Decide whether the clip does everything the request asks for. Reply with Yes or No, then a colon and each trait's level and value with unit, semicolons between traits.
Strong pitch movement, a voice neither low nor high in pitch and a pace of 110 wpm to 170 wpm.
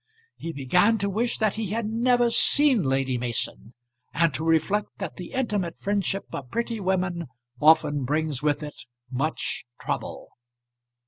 Yes: wide, 6.3 semitones; medium, 180 Hz; average, 145 wpm